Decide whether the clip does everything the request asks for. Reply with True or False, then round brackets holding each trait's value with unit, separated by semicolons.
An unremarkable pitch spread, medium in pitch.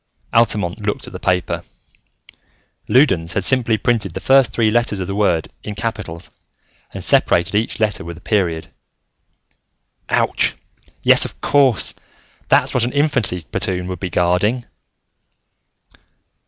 False (4.7 semitones; 105 Hz)